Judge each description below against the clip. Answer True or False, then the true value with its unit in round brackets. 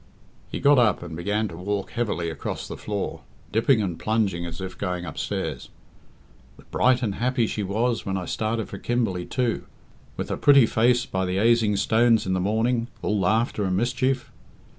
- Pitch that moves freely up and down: False (4.1 semitones)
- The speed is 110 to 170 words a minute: False (185 wpm)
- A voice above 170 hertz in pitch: False (110 Hz)